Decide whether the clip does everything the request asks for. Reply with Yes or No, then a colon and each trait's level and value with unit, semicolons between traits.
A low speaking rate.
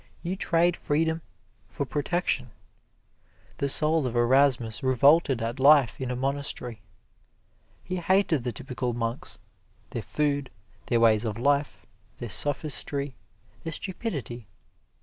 Yes: slow, 120 wpm